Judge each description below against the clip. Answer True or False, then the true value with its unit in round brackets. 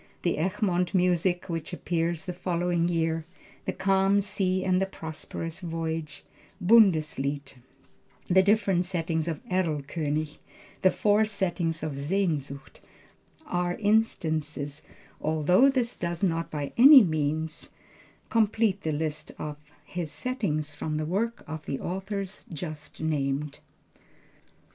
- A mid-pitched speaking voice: True (170 Hz)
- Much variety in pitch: False (3.6 semitones)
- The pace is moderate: False (115 wpm)